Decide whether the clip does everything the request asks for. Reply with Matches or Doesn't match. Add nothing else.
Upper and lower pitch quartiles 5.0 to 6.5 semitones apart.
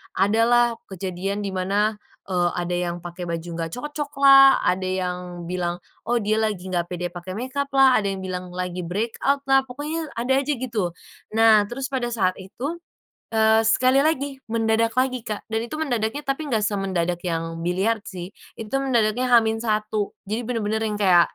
Matches